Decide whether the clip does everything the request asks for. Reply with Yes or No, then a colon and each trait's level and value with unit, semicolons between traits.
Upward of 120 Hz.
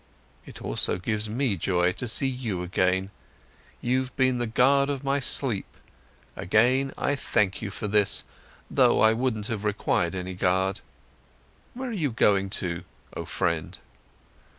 No: low, 110 Hz